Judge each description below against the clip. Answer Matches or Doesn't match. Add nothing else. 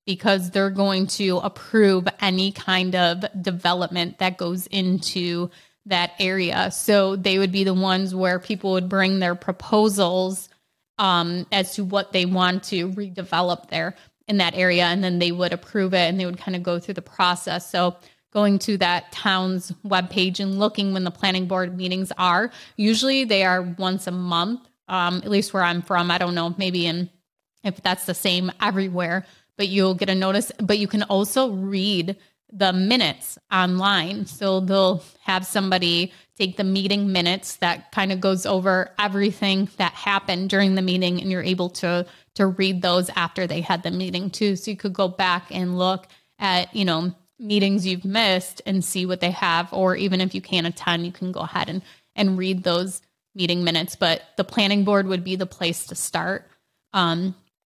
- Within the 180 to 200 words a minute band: Matches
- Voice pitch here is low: Doesn't match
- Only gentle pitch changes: Matches